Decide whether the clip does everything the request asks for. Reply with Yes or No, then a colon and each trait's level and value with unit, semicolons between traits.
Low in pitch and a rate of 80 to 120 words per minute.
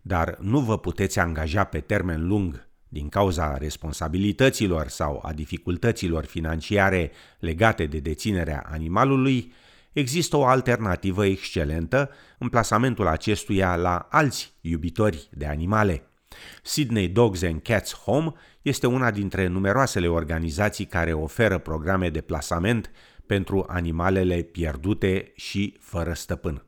Yes: very low, 95 Hz; slow, 115 wpm